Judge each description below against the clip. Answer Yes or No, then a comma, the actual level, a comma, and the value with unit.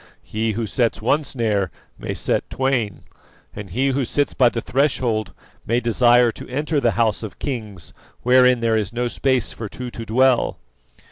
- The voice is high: No, low, 120 Hz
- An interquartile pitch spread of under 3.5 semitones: Yes, average, 2.8 semitones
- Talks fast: No, average, 175 wpm